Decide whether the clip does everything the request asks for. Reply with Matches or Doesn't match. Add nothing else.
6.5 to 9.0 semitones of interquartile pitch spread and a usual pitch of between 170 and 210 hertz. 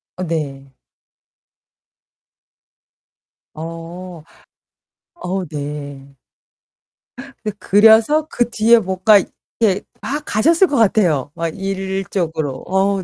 Doesn't match